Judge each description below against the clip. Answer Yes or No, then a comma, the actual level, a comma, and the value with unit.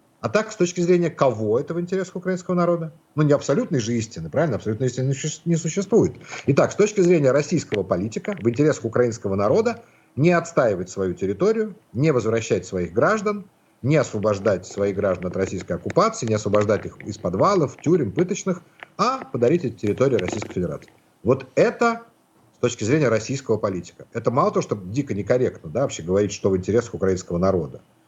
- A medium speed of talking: No, fast, 170 wpm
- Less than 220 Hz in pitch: Yes, low, 135 Hz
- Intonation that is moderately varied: No, wide, 8.7 semitones